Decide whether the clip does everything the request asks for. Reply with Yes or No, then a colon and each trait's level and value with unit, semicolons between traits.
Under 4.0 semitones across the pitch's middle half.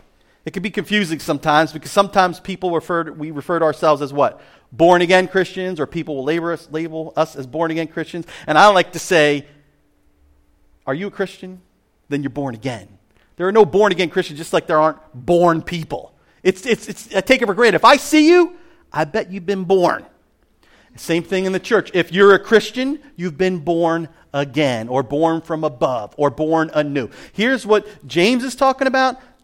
No: average, 4.5 semitones